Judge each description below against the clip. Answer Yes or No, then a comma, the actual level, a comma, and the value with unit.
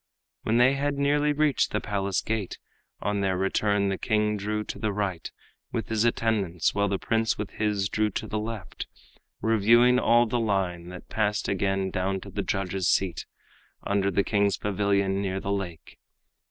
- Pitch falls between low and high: No, low, 100 Hz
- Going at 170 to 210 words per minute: Yes, average, 175 wpm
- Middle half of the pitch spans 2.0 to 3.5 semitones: Yes, narrow, 2.4 semitones